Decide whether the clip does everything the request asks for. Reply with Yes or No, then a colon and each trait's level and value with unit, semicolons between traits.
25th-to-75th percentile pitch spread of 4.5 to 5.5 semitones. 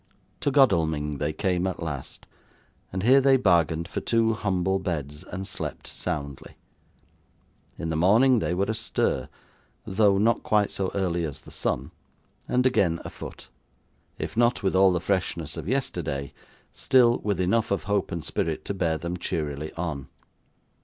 Yes: average, 4.8 semitones